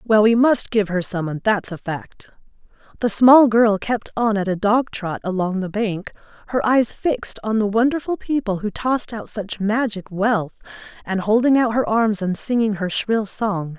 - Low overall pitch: No, high, 210 Hz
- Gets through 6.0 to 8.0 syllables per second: No, 4.6 syllables/s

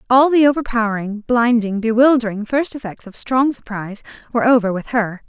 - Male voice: No, female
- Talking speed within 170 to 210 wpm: No, average, 160 wpm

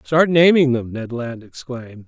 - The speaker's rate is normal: Yes, average, 175 wpm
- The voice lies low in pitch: Yes, low, 130 Hz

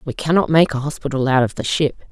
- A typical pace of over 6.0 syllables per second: Yes, 6.5 syllables/s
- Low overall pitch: No, medium, 145 Hz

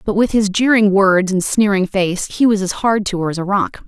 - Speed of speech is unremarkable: No, fast, 265 wpm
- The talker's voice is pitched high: Yes, high, 195 Hz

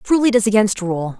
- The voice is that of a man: No, female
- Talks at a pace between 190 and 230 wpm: No, fast, 250 wpm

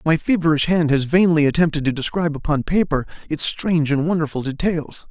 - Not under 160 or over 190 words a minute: Yes, average, 175 wpm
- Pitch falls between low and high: Yes, medium, 160 Hz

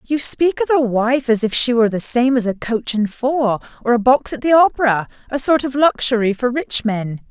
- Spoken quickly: Yes, fast, 230 wpm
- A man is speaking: No, female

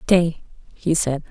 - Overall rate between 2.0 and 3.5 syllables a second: Yes, 3.3 syllables/s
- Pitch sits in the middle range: Yes, medium, 160 Hz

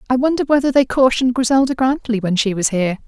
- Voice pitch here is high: Yes, high, 245 Hz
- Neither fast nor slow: No, fast, 215 wpm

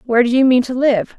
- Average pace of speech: No, fast, 305 wpm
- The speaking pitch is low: No, high, 245 Hz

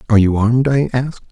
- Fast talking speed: Yes, fast, 230 wpm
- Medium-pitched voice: No, low, 120 Hz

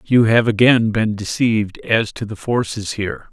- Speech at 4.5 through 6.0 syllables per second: Yes, 4.7 syllables/s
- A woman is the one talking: No, male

